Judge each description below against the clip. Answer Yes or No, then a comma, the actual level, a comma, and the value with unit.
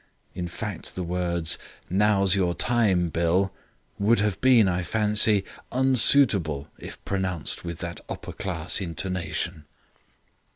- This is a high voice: No, very low, 95 Hz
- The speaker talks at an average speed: No, slow, 120 wpm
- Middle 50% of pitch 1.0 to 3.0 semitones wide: No, average, 3.4 semitones